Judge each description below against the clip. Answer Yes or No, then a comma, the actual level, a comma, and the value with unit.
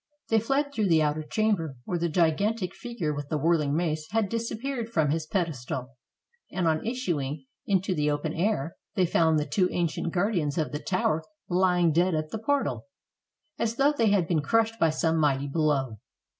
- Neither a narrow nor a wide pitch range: No, wide, 5.7 semitones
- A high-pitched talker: No, medium, 170 Hz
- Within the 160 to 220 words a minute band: Yes, average, 185 wpm